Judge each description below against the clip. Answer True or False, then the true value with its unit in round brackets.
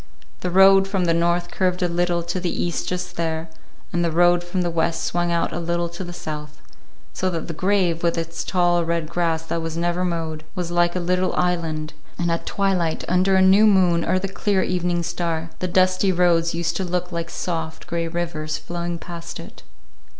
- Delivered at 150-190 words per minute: False (205 wpm)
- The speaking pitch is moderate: True (175 Hz)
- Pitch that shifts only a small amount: True (1.4 semitones)